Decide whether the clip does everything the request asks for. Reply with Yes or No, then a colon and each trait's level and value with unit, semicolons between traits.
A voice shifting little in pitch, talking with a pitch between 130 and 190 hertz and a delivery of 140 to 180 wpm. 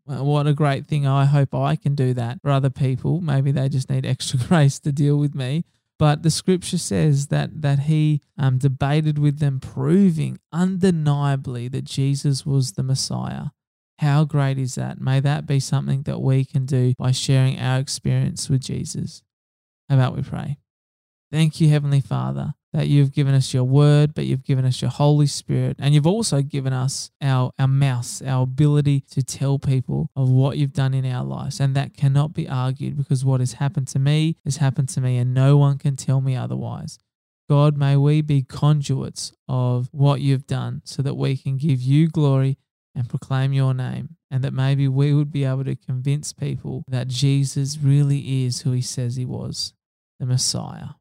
No: narrow, 1.8 semitones; medium, 140 Hz; average, 190 wpm